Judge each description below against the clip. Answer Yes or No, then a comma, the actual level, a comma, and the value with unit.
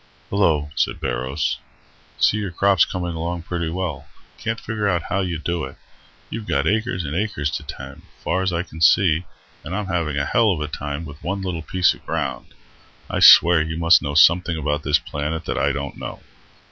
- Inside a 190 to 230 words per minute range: Yes, average, 195 wpm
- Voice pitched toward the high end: No, very low, 85 Hz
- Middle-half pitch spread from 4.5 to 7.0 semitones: No, average, 3.8 semitones